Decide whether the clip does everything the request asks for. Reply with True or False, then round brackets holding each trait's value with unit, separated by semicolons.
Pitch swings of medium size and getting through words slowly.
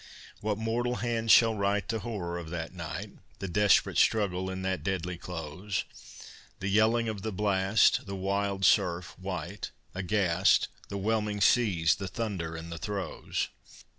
False (3.0 semitones; 150 wpm)